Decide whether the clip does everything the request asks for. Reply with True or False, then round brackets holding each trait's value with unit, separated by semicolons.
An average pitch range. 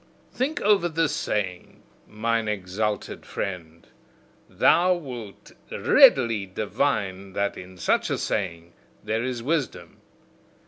False (6.2 semitones)